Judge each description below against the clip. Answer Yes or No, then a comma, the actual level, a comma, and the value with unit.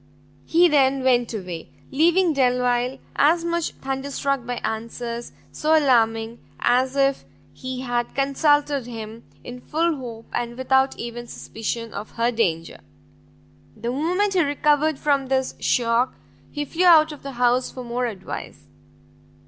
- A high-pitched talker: Yes, very high, 260 Hz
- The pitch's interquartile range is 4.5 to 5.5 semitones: No, average, 3.6 semitones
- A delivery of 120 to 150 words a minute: Yes, average, 140 wpm